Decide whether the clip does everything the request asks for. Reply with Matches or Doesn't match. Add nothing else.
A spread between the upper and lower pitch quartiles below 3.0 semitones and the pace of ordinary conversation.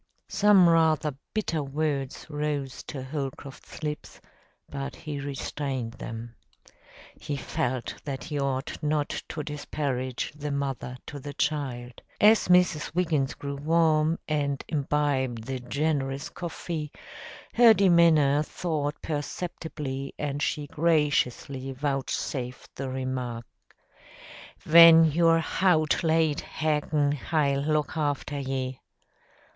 Doesn't match